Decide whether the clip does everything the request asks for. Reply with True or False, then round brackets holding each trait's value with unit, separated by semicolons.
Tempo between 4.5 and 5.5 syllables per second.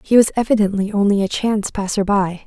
False (6.2 syllables/s)